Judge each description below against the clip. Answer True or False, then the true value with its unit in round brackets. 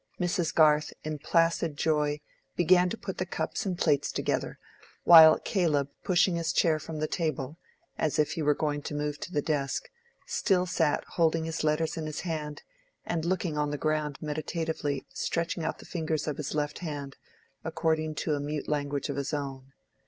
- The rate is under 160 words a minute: False (180 wpm)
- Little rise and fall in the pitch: True (2.1 semitones)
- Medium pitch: True (155 Hz)